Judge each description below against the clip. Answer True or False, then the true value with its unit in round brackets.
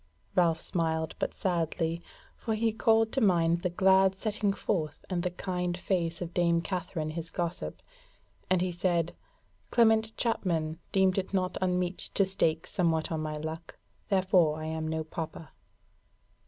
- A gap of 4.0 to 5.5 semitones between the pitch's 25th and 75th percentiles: False (2.7 semitones)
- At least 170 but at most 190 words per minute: False (155 wpm)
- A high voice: False (175 Hz)